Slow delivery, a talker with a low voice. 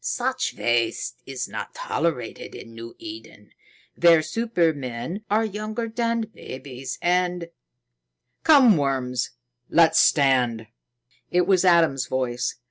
No: slow, 115 wpm; medium, 165 Hz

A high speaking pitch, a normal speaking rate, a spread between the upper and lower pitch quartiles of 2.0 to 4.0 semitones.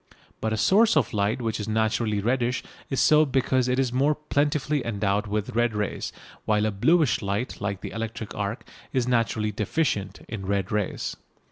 No: low, 115 Hz; average, 175 wpm; average, 3.7 semitones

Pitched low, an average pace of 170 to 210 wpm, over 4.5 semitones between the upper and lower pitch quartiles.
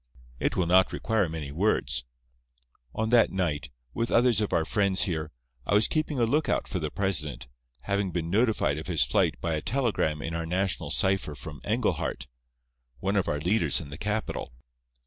Yes: very low, 95 Hz; average, 180 wpm; wide, 5.4 semitones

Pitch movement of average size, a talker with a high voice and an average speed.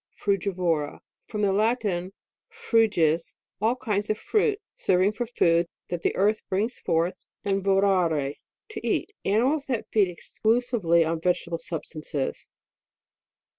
No: average, 4.7 semitones; high, 195 Hz; slow, 125 wpm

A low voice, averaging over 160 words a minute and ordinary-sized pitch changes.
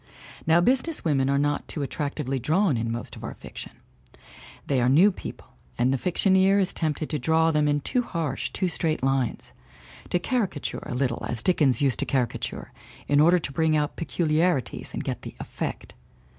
No: medium, 150 Hz; average, 185 wpm; average, 4.5 semitones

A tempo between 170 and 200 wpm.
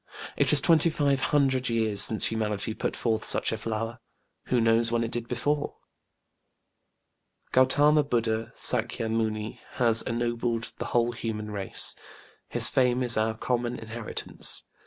No: average, 140 wpm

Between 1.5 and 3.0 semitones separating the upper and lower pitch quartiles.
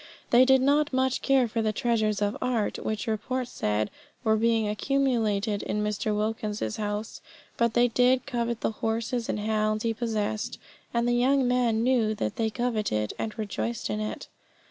Yes: narrow, 2.5 semitones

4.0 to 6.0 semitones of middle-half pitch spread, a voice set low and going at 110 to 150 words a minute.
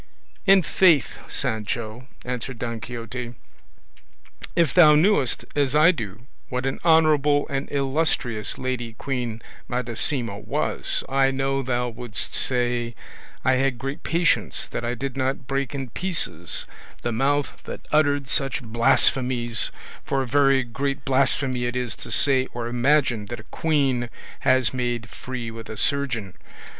No: average, 2.8 semitones; low, 130 Hz; average, 140 wpm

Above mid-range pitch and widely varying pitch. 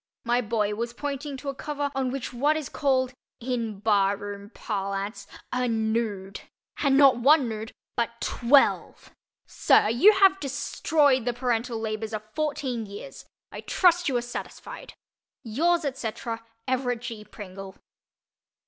No: high, 240 Hz; average, 4.1 semitones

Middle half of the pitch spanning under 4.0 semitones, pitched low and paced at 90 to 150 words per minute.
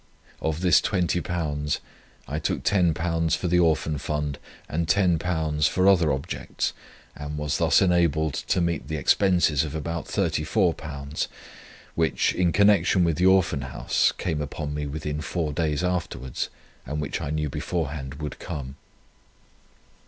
Yes: average, 2.8 semitones; very low, 80 Hz; average, 145 wpm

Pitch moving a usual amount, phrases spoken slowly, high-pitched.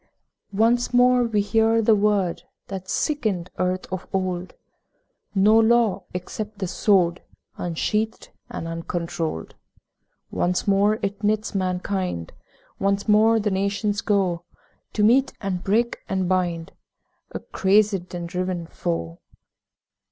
Yes: average, 3.1 semitones; slow, 120 wpm; high, 195 Hz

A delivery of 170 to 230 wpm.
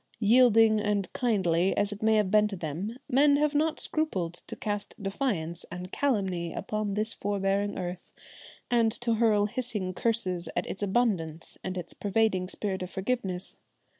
No: average, 160 wpm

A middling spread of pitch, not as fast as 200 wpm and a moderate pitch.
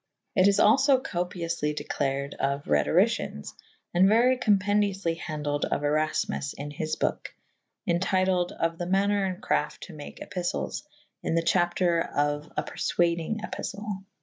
Yes: average, 4.8 semitones; average, 150 wpm; medium, 175 Hz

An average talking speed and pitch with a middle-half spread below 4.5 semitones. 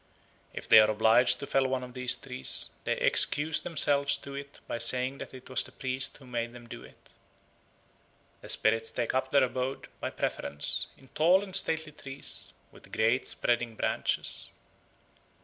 Yes: average, 170 wpm; average, 2.9 semitones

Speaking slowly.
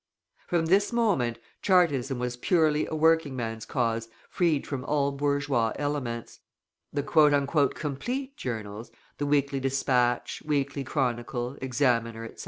Yes: slow, 120 wpm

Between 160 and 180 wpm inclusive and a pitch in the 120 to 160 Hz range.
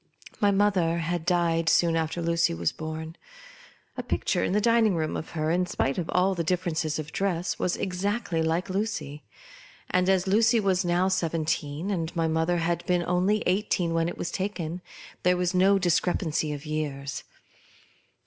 No: average, 175 wpm; medium, 175 Hz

